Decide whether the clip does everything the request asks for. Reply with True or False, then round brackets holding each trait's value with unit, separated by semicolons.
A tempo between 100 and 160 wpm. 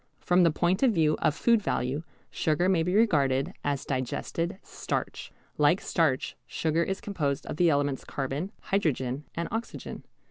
True (155 wpm)